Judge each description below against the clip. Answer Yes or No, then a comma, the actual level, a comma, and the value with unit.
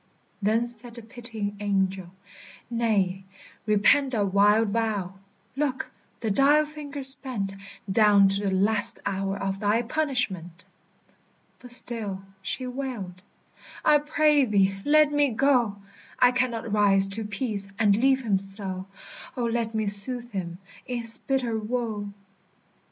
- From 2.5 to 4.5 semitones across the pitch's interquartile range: Yes, average, 4.1 semitones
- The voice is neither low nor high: No, high, 220 Hz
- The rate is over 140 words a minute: No, slow, 135 wpm